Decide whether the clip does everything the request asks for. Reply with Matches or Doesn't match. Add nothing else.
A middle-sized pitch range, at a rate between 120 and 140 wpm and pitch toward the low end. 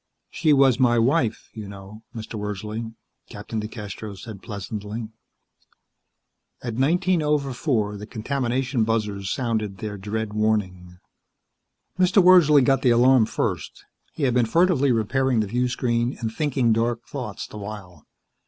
Matches